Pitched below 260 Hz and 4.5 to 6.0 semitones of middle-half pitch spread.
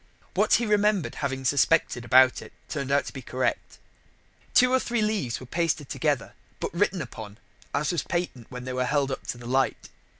Yes: medium, 140 Hz; wide, 5.4 semitones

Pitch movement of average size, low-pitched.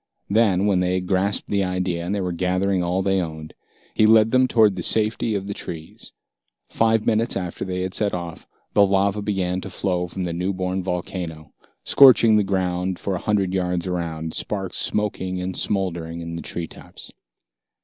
No: narrow, 2.1 semitones; very low, 95 Hz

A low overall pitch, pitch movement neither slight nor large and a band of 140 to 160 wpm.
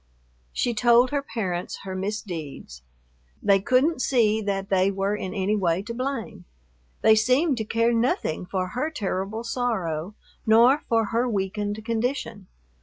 No: high, 215 Hz; average, 3.8 semitones; average, 145 wpm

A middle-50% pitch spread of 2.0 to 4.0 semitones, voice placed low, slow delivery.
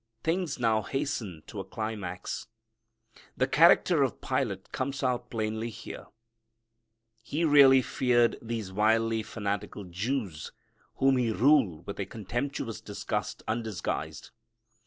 No: average, 4.4 semitones; low, 115 Hz; slow, 115 wpm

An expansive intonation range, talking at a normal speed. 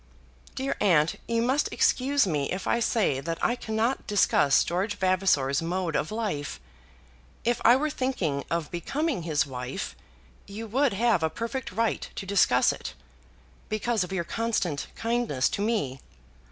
Yes: wide, 6.4 semitones; average, 155 wpm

